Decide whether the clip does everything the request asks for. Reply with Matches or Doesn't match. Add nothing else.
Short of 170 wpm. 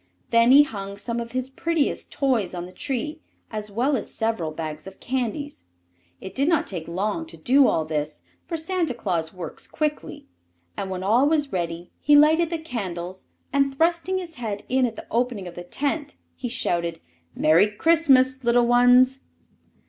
Doesn't match